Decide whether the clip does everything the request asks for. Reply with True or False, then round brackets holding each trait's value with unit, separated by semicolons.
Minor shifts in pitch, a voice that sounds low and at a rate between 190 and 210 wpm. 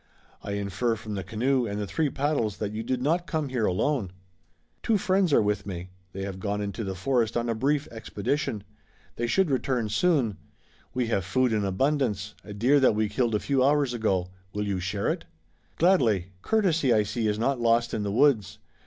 False (5.1 semitones; 115 Hz; 200 wpm)